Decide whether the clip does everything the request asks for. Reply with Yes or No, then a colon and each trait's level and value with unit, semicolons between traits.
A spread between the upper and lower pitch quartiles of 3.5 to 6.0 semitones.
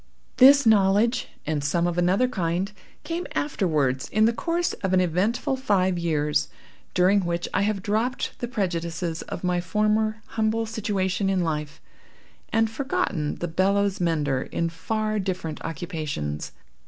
Yes: average, 4.5 semitones